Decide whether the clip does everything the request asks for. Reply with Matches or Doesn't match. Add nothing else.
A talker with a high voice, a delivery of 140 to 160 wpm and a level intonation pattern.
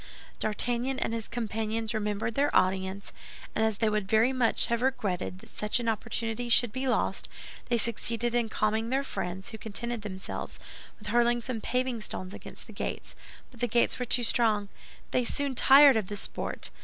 Doesn't match